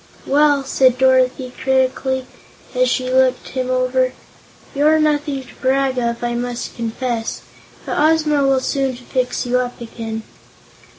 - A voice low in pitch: No, very high, 260 Hz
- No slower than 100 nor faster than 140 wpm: Yes, slow, 135 wpm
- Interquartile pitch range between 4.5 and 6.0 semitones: No, narrow, 1.6 semitones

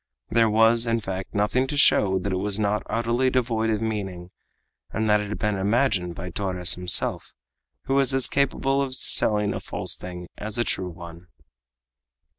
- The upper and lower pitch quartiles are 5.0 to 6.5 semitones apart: No, average, 3.9 semitones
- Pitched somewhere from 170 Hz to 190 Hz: No, low, 105 Hz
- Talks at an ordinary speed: Yes, average, 180 wpm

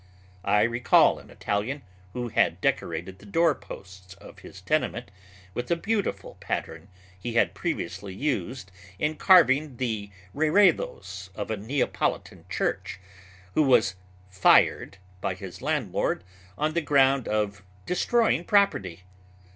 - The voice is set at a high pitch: No, low, 120 Hz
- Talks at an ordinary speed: No, slow, 125 wpm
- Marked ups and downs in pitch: Yes, wide, 7.4 semitones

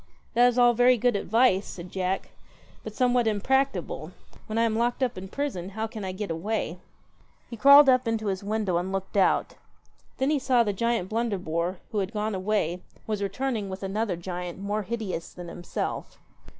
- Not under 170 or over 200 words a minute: Yes, average, 190 wpm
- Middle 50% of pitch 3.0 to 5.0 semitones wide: Yes, average, 4.1 semitones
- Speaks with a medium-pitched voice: No, high, 210 Hz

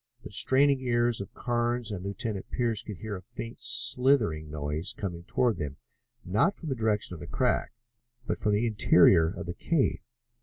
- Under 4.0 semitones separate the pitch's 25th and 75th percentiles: No, average, 5.0 semitones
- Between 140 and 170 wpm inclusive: No, average, 180 wpm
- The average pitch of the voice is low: Yes, low, 110 Hz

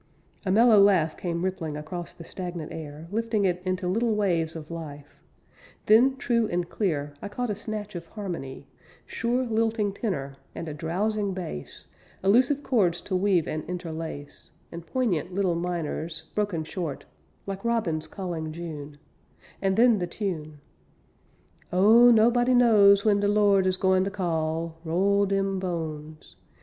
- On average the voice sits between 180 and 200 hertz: Yes, medium, 185 Hz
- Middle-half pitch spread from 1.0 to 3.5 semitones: No, average, 4.3 semitones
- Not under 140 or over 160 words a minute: Yes, average, 150 wpm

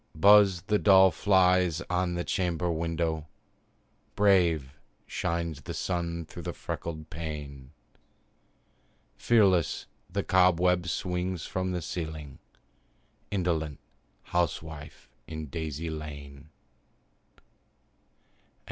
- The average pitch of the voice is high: No, very low, 85 Hz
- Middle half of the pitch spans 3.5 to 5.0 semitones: No, average, 2.7 semitones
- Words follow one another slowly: Yes, slow, 95 wpm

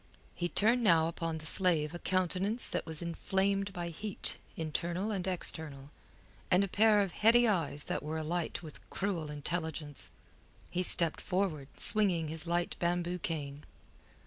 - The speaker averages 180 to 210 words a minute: No, average, 150 wpm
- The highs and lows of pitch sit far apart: No, average, 3.3 semitones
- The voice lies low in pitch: No, medium, 175 Hz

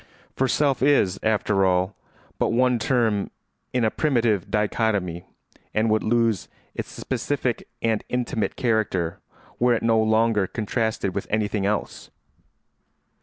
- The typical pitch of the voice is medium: No, low, 110 Hz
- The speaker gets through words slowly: Yes, slow, 125 wpm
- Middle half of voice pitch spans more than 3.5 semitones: No, narrow, 2.5 semitones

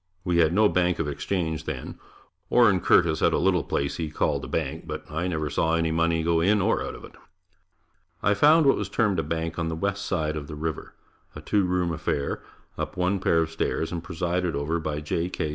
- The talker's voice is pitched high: No, very low, 85 Hz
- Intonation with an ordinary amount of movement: No, narrow, 2.3 semitones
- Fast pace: Yes, fast, 220 wpm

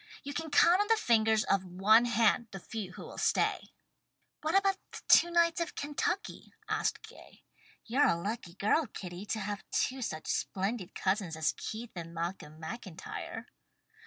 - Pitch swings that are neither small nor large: No, wide, 7.5 semitones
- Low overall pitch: No, high, 220 Hz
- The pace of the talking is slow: No, average, 165 wpm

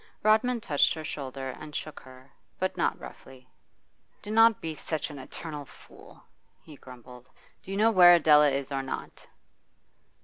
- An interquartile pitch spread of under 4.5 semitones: No, average, 5.1 semitones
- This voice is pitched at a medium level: Yes, medium, 150 Hz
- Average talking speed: Yes, average, 160 wpm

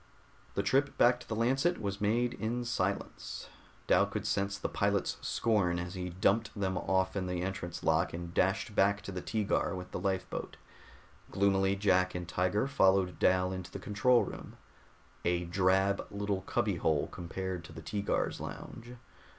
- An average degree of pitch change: No, narrow, 2.2 semitones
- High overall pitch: No, very low, 95 Hz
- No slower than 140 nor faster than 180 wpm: Yes, average, 165 wpm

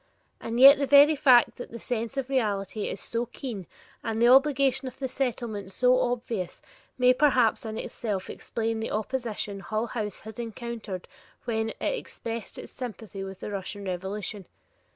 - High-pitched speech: Yes, high, 230 Hz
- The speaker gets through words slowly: No, average, 165 wpm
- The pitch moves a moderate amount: Yes, average, 3.4 semitones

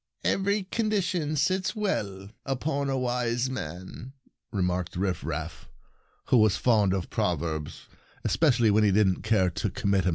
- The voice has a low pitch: Yes, low, 110 Hz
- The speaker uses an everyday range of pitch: No, wide, 7.0 semitones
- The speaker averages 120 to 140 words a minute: No, average, 155 wpm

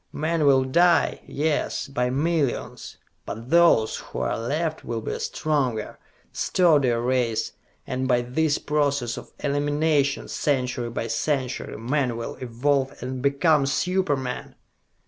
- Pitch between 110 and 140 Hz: Yes, low, 135 Hz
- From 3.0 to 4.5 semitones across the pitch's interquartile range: Yes, average, 3.4 semitones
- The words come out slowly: Yes, slow, 130 wpm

